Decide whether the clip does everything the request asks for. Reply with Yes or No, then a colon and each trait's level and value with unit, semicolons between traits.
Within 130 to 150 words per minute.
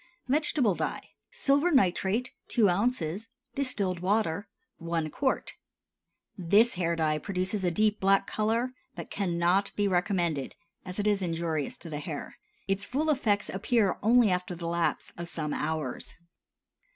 Yes: average, 140 wpm